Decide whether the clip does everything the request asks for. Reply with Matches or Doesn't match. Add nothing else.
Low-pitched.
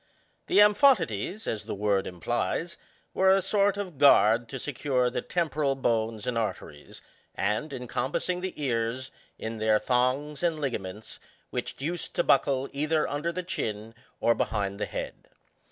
Matches